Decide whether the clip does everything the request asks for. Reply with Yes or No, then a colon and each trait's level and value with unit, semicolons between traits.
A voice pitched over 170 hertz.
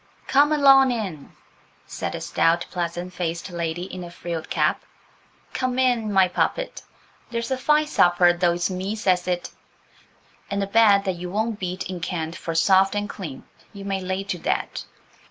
Yes: medium, 185 Hz